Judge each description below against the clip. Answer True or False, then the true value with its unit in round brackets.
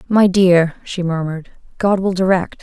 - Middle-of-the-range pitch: True (180 Hz)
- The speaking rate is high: False (160 wpm)